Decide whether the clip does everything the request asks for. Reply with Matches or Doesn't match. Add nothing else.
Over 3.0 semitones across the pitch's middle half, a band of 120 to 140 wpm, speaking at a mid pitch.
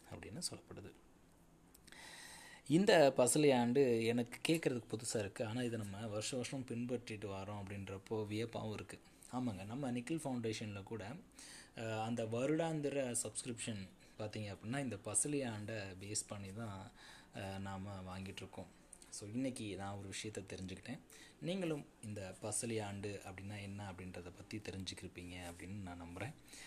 Doesn't match